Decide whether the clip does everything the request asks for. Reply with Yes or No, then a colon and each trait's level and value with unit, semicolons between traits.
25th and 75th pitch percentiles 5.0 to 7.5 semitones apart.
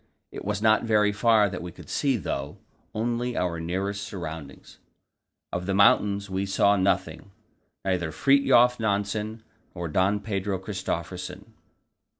No: average, 2.9 semitones